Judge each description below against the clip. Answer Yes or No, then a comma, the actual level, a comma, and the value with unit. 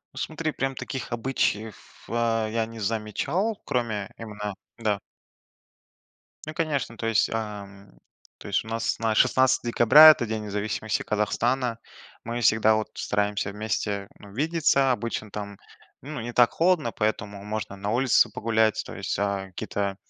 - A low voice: Yes, low, 110 Hz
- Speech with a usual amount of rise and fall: Yes, average, 3.0 semitones